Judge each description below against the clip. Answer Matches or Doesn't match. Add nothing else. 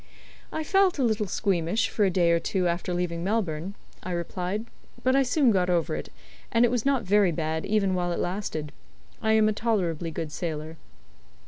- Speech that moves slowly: Doesn't match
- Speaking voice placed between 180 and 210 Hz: Matches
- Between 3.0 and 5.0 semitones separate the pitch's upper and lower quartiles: Matches